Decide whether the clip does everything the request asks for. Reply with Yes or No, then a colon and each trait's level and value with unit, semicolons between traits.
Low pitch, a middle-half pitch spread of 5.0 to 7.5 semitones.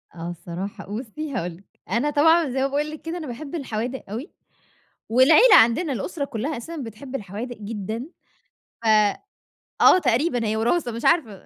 No: very high, 250 Hz; wide, 5.5 semitones